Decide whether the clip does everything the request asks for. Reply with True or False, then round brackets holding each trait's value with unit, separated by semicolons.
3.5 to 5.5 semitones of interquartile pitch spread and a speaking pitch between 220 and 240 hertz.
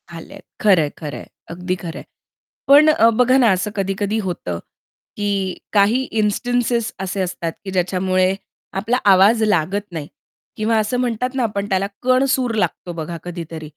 False (4.4 semitones; 200 Hz)